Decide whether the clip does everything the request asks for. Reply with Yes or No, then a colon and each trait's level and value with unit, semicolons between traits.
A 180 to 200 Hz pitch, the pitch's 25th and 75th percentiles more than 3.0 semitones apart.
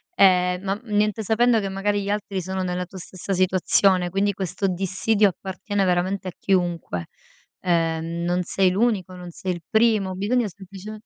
No: high, 190 Hz; narrow, 2.2 semitones